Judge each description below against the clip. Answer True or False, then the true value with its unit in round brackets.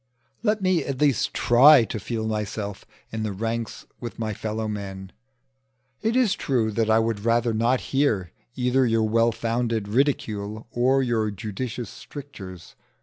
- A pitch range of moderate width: True (3.0 semitones)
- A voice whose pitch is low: True (115 Hz)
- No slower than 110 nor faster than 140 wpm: False (150 wpm)